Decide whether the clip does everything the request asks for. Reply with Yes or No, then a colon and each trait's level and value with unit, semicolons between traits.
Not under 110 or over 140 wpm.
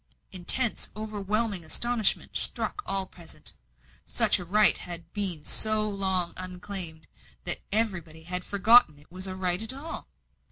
Yes: slow, 135 wpm